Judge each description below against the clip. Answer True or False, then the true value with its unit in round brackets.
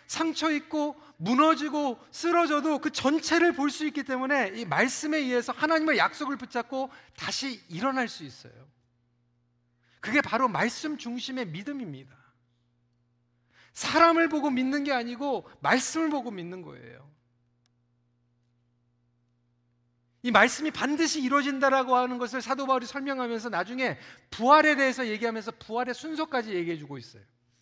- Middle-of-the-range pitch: False (250 Hz)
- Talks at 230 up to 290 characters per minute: False (305 characters per minute)